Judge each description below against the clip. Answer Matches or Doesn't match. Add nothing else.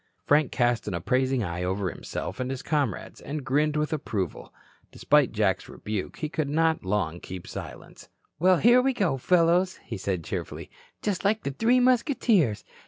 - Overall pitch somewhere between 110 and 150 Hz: Matches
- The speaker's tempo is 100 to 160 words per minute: Doesn't match